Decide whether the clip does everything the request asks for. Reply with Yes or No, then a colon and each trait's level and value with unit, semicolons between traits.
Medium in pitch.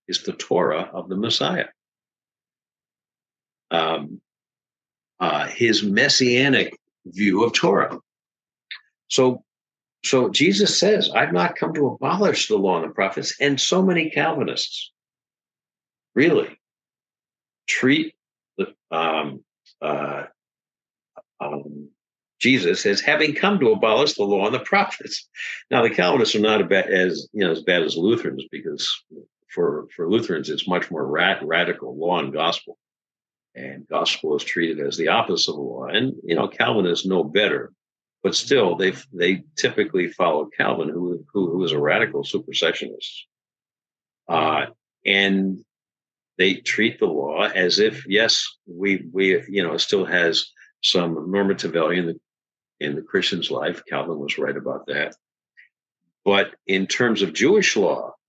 No: low, 125 Hz